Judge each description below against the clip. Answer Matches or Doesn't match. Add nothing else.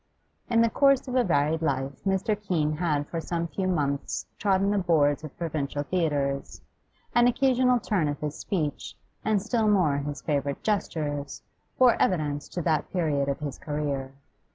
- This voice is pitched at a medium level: Matches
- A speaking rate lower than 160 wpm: Doesn't match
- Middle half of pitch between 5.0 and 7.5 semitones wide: Matches